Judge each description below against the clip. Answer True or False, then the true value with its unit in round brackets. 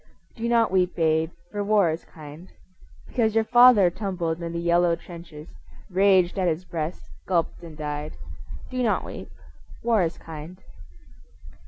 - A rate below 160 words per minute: True (150 wpm)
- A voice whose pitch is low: False (175 Hz)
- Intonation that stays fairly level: False (3.8 semitones)